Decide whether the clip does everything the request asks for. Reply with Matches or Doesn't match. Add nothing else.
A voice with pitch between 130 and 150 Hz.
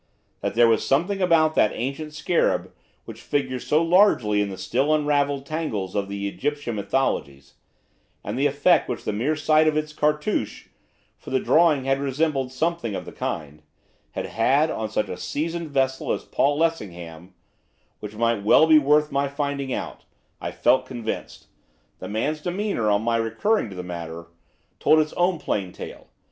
Matches